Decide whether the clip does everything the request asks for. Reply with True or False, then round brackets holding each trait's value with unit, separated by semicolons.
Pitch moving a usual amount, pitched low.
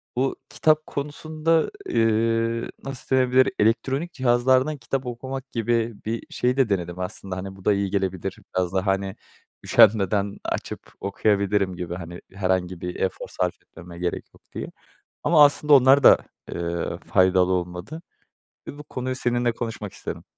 False (5.9 semitones; 110 Hz)